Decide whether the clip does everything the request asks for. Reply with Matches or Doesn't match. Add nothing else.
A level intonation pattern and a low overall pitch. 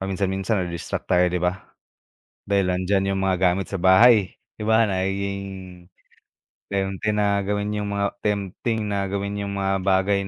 Matches